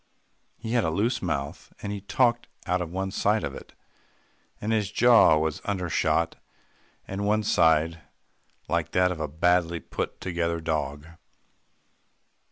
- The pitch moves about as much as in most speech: Yes, average, 4.3 semitones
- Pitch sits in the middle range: No, very low, 90 Hz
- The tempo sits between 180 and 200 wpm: No, average, 145 wpm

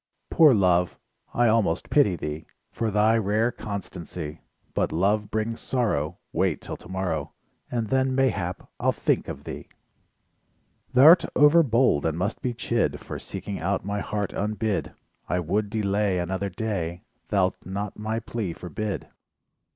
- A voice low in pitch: Yes, low, 105 Hz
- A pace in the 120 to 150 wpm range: Yes, average, 140 wpm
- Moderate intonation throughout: Yes, average, 3.9 semitones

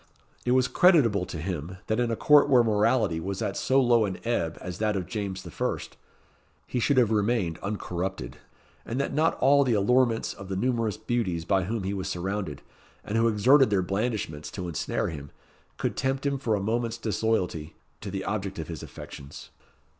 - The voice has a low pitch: Yes, low, 105 Hz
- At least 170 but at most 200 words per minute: Yes, average, 190 wpm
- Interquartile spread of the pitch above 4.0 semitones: Yes, average, 4.5 semitones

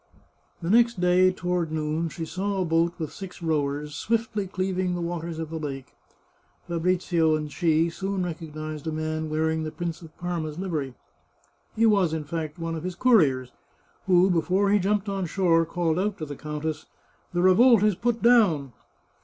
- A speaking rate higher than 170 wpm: Yes, average, 180 wpm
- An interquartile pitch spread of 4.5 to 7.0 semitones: No, average, 3.0 semitones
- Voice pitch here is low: No, medium, 170 Hz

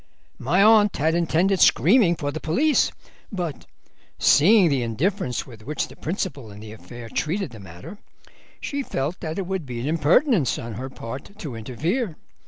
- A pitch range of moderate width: No, wide, 7.8 semitones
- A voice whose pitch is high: No, medium, 155 Hz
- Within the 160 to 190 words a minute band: Yes, average, 170 wpm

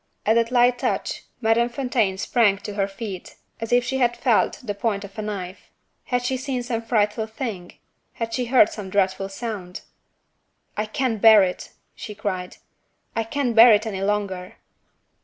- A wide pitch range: No, average, 3.3 semitones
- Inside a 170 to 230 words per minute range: Yes, average, 175 wpm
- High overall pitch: Yes, high, 220 Hz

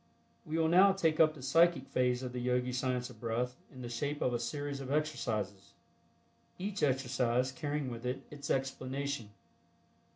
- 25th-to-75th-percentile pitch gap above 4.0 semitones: No, average, 3.0 semitones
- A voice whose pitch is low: Yes, low, 130 Hz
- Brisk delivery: No, average, 170 wpm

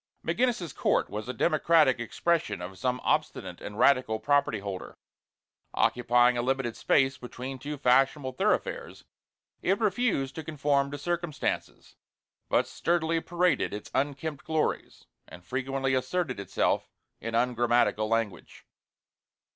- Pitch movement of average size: Yes, average, 4.8 semitones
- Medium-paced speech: No, slow, 125 wpm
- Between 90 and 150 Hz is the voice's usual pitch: Yes, low, 135 Hz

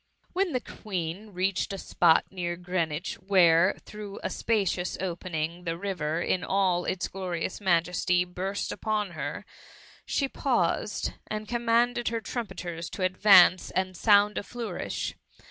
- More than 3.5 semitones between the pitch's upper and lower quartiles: No, average, 3.2 semitones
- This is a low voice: No, medium, 185 Hz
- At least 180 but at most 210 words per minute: No, average, 140 wpm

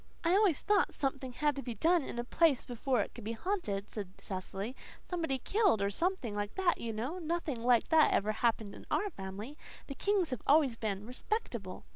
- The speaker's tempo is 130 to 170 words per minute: No, average, 200 wpm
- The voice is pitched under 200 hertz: No, very high, 255 Hz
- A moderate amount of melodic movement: No, wide, 7.7 semitones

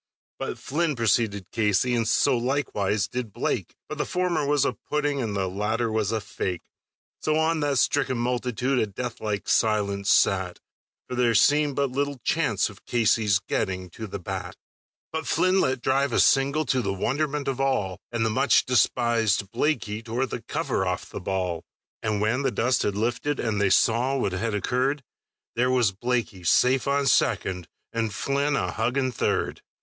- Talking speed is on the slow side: No, average, 175 wpm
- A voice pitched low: Yes, low, 120 Hz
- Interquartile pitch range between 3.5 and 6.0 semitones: Yes, average, 4.8 semitones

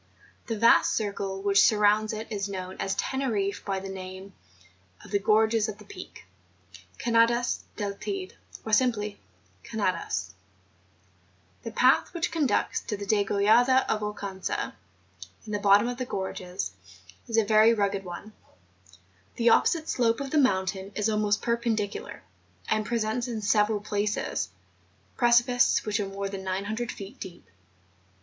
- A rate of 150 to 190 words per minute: No, average, 140 wpm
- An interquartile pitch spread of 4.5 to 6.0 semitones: No, average, 2.7 semitones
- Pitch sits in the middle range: No, high, 210 Hz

